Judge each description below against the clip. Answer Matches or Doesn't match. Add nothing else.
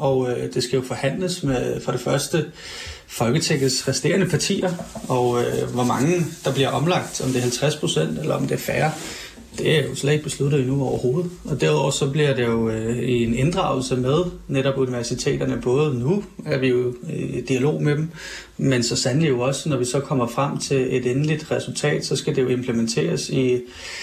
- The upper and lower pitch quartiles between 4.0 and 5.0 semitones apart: Doesn't match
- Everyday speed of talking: Matches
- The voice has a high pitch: Doesn't match